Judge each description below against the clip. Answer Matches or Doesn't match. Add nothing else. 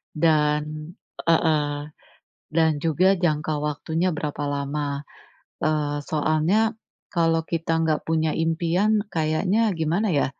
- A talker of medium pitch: Matches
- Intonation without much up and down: Matches